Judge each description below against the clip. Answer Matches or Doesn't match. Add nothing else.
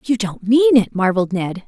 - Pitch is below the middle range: Doesn't match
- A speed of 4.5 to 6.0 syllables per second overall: Matches